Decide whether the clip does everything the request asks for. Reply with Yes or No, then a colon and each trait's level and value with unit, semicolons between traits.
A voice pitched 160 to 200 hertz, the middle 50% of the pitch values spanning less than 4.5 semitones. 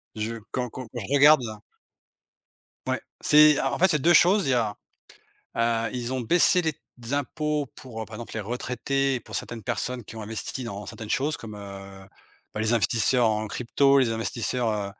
No: low, 120 Hz; average, 3.9 semitones